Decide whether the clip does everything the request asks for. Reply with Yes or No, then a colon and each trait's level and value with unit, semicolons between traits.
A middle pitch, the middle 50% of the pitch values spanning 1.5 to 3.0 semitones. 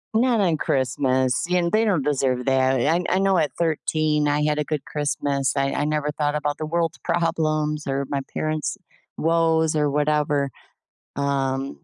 Yes: medium, 150 Hz; narrow, 2.6 semitones